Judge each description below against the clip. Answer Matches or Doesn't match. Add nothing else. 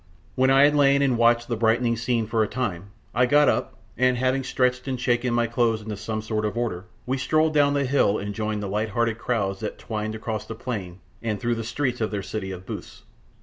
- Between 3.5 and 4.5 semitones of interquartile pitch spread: Doesn't match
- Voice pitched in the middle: Doesn't match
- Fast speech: Matches